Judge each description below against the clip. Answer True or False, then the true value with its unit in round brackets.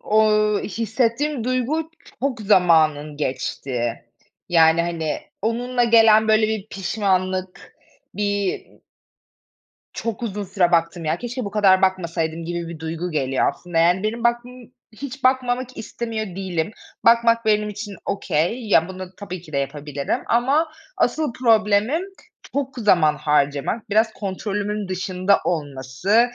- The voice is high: True (200 Hz)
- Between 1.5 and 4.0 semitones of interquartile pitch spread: False (5.5 semitones)